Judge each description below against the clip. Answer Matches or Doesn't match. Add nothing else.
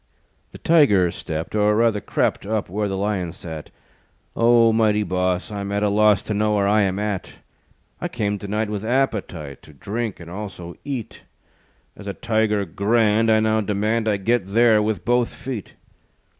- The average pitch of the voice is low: Matches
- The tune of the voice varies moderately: Doesn't match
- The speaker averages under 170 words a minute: Doesn't match